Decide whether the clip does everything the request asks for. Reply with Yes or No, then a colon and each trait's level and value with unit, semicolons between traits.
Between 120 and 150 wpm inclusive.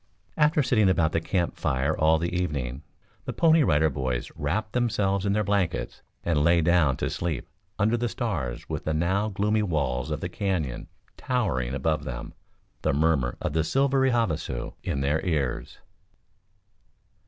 No: average, 160 wpm